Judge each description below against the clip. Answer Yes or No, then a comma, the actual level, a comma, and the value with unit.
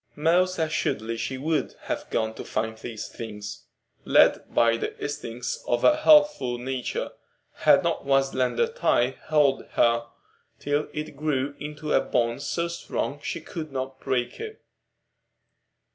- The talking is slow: No, average, 145 wpm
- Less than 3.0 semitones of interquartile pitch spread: No, average, 4.5 semitones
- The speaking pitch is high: No, low, 135 Hz